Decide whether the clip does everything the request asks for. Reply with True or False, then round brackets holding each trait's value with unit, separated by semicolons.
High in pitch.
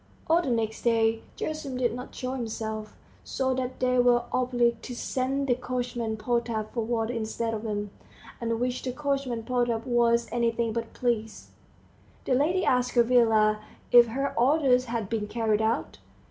True (240 Hz)